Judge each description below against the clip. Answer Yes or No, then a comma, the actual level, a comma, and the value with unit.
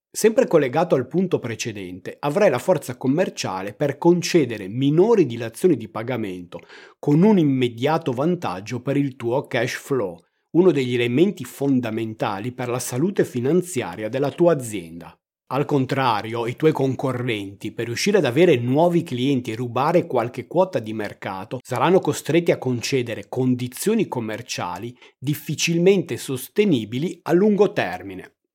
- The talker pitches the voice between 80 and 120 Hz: No, low, 130 Hz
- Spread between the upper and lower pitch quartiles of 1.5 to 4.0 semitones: No, wide, 5.5 semitones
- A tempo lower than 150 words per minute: Yes, average, 130 wpm